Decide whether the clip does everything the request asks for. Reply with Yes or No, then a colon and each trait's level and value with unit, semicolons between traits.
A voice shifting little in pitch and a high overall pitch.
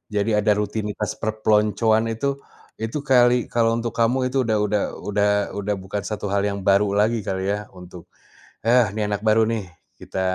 No: narrow, 1.8 semitones; low, 110 Hz